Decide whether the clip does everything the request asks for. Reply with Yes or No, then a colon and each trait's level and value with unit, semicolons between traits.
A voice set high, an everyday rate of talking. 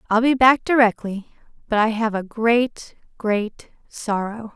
Yes: high, 225 Hz; average, 145 wpm